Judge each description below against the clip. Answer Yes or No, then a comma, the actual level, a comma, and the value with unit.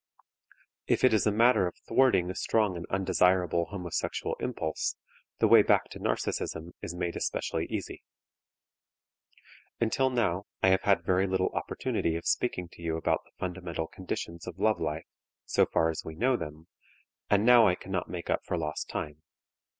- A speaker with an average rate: Yes, average, 170 wpm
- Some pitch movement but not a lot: Yes, average, 3.3 semitones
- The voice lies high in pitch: No, very low, 90 Hz